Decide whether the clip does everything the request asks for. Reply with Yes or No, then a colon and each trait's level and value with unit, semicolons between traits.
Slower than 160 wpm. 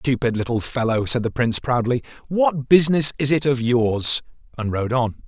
No: average, 180 wpm